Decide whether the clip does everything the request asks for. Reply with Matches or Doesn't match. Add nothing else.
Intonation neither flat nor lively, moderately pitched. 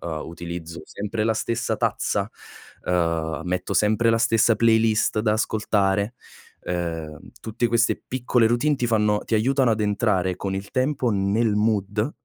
Doesn't match